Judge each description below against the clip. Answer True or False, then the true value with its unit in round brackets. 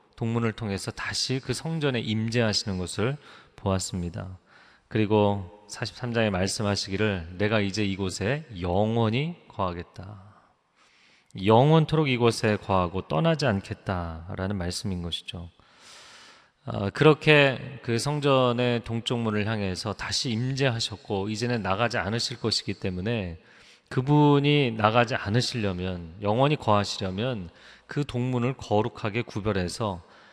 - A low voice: True (110 Hz)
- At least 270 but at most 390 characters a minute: True (280 characters per minute)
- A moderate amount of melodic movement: True (4.0 semitones)